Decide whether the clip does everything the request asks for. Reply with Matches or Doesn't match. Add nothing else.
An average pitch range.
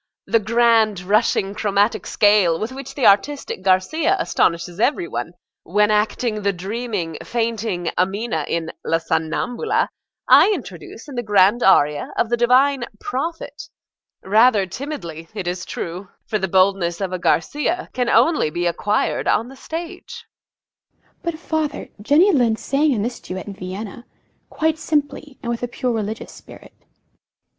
Doesn't match